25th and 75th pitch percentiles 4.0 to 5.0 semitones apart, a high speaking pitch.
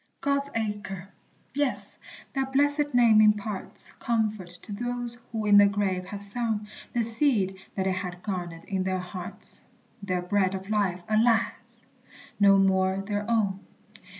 No: average, 3.3 semitones; high, 205 Hz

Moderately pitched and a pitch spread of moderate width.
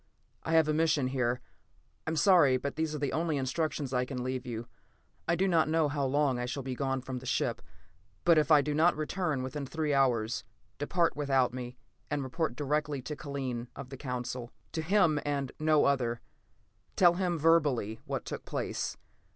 Yes: medium, 145 Hz; average, 3.5 semitones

